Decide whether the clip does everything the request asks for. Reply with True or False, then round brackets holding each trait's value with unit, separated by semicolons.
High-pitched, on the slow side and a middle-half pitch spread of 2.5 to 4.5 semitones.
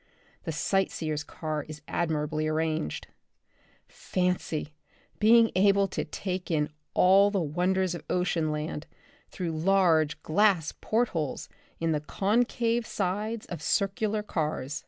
False (175 Hz; 125 wpm; 4.2 semitones)